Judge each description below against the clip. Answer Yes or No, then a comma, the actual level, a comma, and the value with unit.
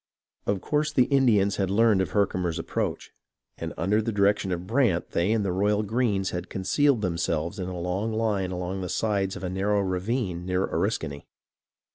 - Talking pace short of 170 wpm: No, average, 185 wpm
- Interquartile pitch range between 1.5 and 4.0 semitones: Yes, average, 3.1 semitones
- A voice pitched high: No, very low, 95 Hz